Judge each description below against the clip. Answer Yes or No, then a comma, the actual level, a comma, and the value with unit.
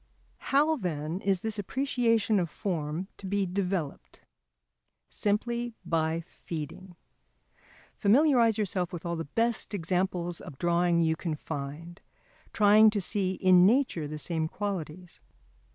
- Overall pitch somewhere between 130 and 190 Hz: Yes, medium, 185 Hz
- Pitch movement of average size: Yes, average, 4.2 semitones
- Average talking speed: No, slow, 125 wpm